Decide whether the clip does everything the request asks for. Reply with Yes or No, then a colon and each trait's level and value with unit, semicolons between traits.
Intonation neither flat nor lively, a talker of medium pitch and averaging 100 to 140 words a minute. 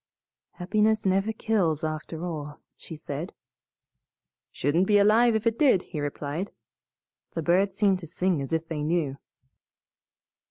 Yes: average, 4.7 semitones; medium, 175 Hz; slow, 135 wpm